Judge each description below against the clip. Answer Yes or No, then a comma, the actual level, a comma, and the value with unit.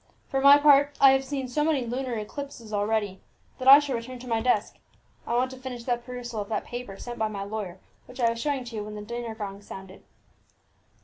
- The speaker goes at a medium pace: No, fast, 230 wpm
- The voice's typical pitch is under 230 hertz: No, high, 240 Hz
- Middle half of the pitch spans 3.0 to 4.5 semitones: Yes, average, 3.7 semitones